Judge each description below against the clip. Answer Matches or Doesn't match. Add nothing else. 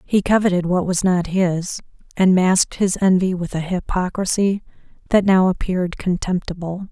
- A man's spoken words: Doesn't match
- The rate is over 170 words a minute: Doesn't match